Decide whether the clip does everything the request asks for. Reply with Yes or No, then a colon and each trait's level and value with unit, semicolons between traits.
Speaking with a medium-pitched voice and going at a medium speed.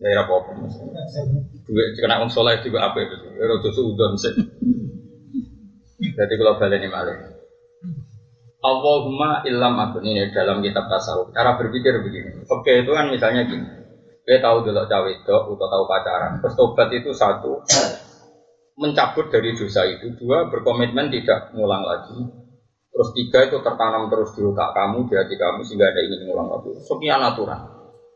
No: medium, 150 Hz; fast, 155 wpm